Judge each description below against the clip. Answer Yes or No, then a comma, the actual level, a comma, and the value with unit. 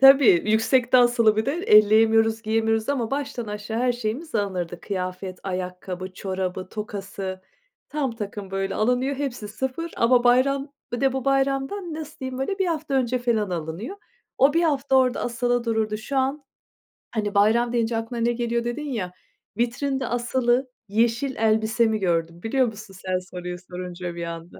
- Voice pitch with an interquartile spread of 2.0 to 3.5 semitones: No, average, 4.6 semitones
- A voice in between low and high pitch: No, high, 230 Hz